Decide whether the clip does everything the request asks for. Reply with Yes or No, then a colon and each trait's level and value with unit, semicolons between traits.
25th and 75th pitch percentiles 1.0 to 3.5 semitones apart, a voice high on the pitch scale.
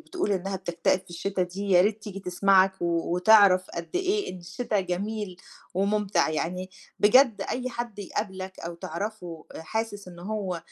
Yes: average, 2.9 semitones; high, 195 Hz